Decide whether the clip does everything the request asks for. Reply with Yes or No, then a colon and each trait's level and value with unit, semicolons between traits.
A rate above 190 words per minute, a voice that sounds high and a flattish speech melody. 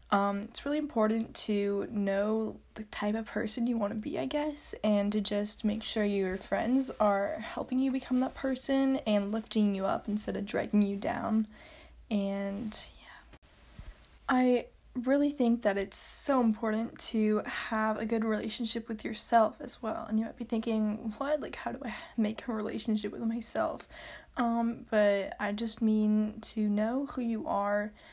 No: average, 175 wpm; high, 220 Hz; narrow, 2.3 semitones